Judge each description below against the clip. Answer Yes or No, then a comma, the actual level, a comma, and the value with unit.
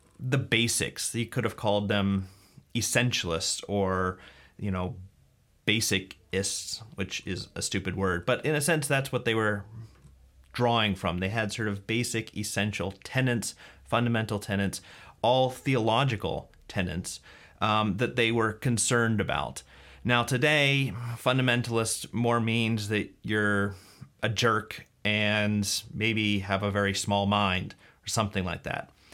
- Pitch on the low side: Yes, low, 105 Hz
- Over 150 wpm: No, slow, 135 wpm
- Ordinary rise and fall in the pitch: Yes, average, 3.3 semitones